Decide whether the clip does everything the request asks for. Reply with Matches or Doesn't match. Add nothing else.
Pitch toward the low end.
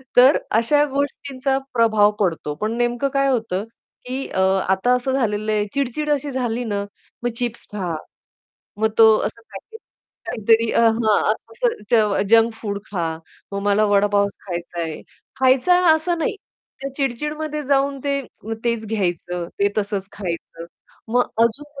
Doesn't match